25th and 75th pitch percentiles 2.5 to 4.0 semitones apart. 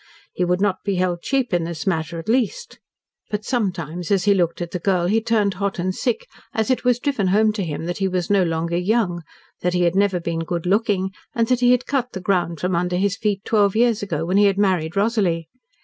Yes: average, 3.6 semitones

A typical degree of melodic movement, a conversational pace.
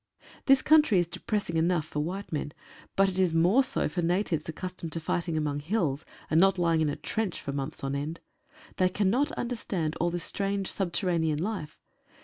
Yes: average, 3.8 semitones; average, 185 wpm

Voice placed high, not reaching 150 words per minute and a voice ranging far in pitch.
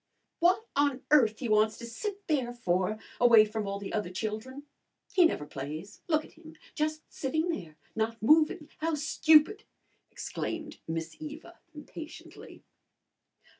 Yes: very high, 265 Hz; average, 140 wpm; wide, 6.6 semitones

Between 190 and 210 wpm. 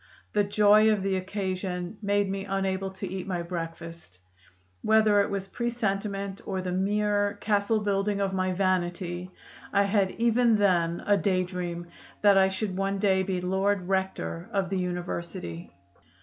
No: average, 155 wpm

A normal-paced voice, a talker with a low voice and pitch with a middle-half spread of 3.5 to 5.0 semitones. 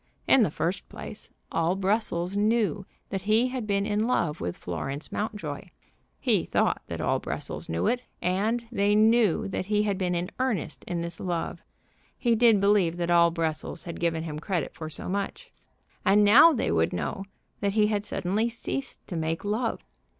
No: average, 180 wpm; high, 200 Hz; average, 4.2 semitones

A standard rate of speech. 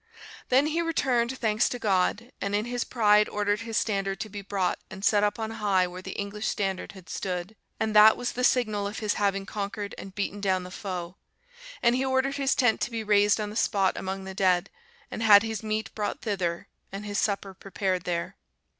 No: fast, 210 wpm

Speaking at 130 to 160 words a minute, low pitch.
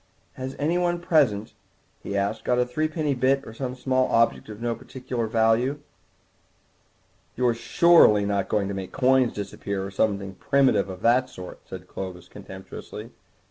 Yes: average, 155 wpm; low, 115 Hz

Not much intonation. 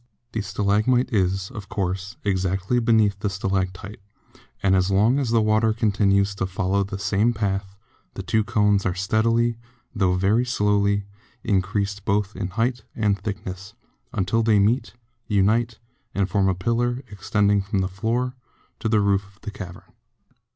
Yes: narrow, 2.3 semitones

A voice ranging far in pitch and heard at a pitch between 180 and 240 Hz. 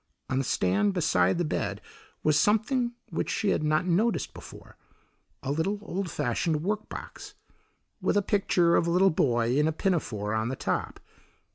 No: wide, 7.2 semitones; medium, 165 Hz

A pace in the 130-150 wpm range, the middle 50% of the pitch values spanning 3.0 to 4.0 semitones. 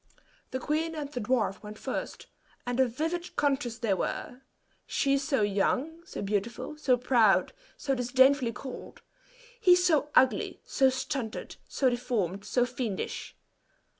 Yes: slow, 135 wpm; average, 3.7 semitones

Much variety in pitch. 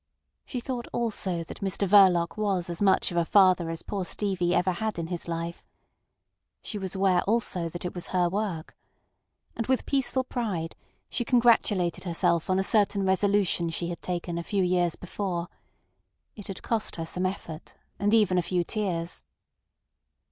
No: average, 3.1 semitones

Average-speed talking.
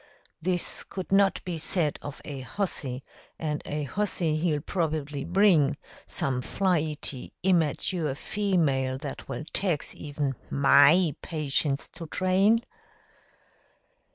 No: slow, 110 wpm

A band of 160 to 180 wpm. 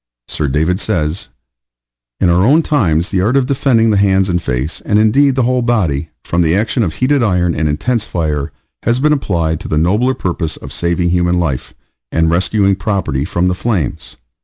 No: average, 190 wpm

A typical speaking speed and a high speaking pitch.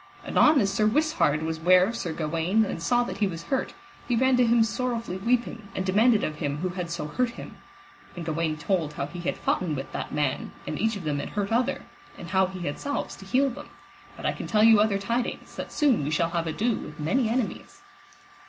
No: fast, 230 wpm; high, 195 Hz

